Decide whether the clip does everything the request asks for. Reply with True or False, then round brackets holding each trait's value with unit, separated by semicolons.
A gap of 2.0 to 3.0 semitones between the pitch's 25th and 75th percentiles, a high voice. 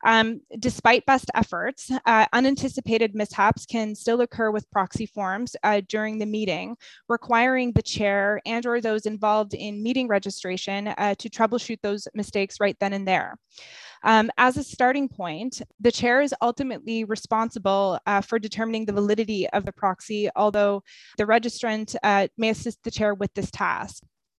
True (2.6 semitones; 220 Hz)